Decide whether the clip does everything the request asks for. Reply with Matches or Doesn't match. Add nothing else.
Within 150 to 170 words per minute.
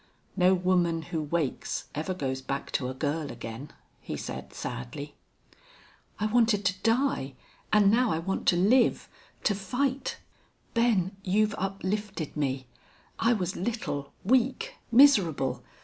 Doesn't match